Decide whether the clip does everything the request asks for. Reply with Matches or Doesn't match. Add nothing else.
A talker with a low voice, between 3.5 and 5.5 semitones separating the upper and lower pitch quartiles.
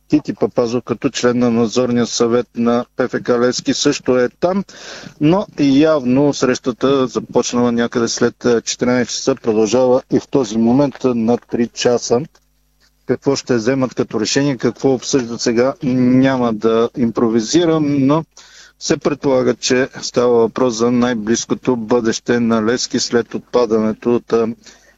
Doesn't match